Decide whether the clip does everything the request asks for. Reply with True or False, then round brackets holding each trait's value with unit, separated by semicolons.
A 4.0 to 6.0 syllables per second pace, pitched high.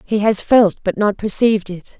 True (5.0 syllables/s; 205 Hz)